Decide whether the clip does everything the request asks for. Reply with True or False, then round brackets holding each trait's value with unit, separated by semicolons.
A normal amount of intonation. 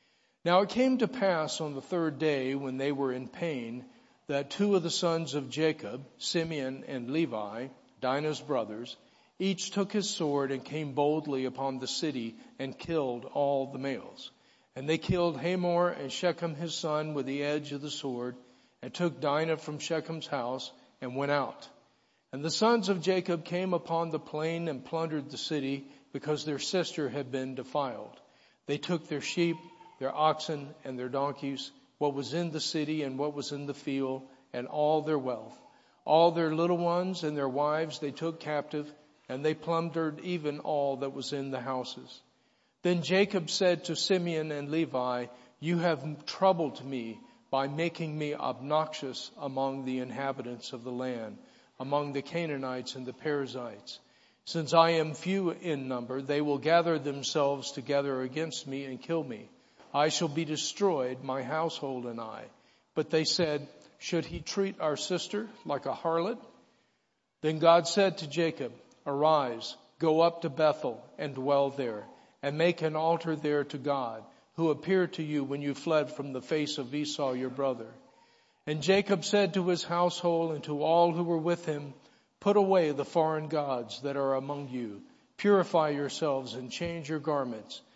True (3.4 semitones)